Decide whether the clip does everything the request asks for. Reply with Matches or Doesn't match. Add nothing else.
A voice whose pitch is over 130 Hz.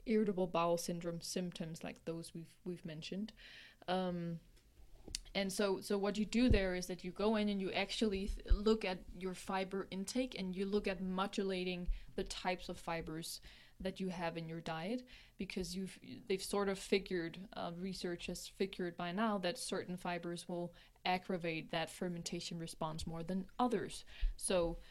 Matches